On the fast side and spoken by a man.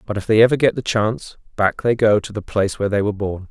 Yes: fast, 290 wpm; male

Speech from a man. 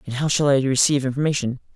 Yes: male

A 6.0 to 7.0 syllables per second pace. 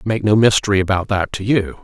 Yes: 6.5 syllables/s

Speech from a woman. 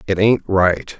No: male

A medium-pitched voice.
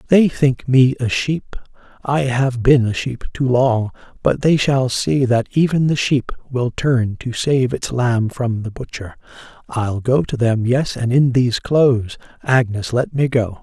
No: low, 125 Hz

